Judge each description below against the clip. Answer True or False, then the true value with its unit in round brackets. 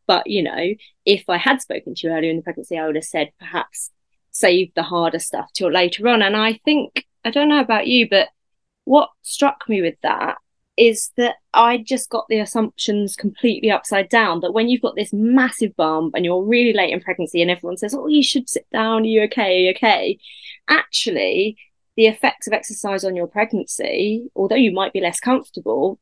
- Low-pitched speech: False (215 Hz)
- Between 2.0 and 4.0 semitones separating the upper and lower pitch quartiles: False (4.7 semitones)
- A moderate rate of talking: False (210 wpm)